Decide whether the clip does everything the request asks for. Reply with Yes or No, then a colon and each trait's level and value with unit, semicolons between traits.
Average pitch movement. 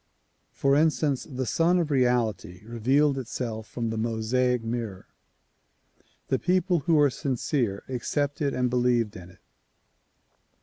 Yes: average, 3.9 semitones